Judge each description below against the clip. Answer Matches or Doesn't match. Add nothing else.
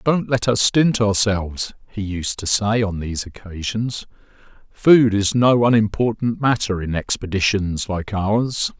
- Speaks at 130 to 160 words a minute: Matches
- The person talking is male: Matches